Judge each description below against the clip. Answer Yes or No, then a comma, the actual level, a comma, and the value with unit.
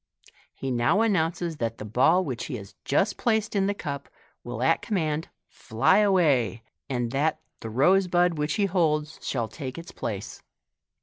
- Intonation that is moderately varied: No, wide, 6.7 semitones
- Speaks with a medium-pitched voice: Yes, medium, 150 Hz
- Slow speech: No, average, 170 wpm